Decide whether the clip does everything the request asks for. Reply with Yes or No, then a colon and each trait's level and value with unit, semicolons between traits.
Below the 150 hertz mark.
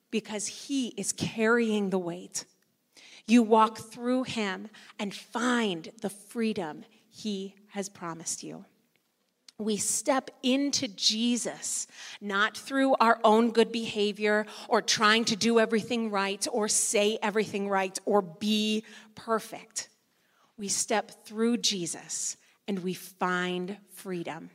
No: high, 215 Hz